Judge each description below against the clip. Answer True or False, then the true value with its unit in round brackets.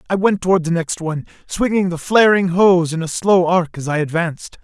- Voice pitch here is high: False (175 Hz)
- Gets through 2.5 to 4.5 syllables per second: False (5.5 syllables/s)